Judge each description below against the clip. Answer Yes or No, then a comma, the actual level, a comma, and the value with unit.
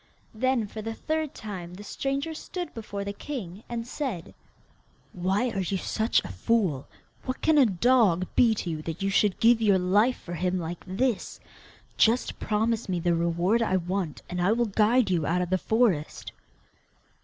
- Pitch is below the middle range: No, high, 205 Hz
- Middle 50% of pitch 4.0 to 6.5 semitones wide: Yes, average, 4.6 semitones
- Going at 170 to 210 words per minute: Yes, average, 180 wpm